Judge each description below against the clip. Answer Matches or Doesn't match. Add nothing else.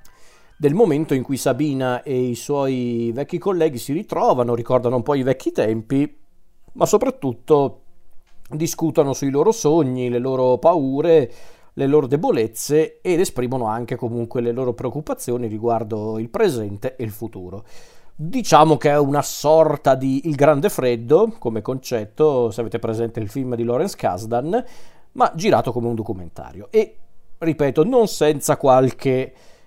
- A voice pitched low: Matches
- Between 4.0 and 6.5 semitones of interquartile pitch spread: Matches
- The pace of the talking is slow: Doesn't match